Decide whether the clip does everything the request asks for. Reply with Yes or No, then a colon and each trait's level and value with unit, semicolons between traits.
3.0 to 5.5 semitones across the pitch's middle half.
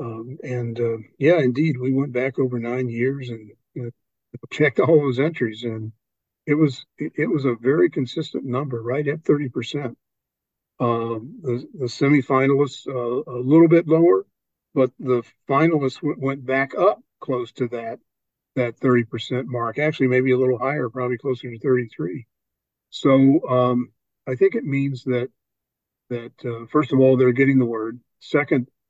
No: narrow, 2.4 semitones